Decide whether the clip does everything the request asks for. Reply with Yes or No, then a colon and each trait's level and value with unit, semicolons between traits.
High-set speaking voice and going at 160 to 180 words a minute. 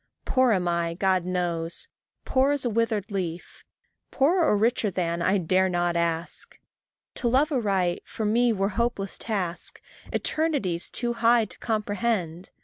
No: high, 200 Hz; average, 145 wpm